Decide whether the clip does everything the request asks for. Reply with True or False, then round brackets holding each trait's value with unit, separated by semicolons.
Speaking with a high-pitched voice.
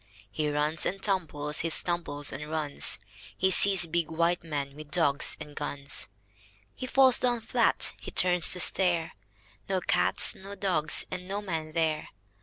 False (165 Hz)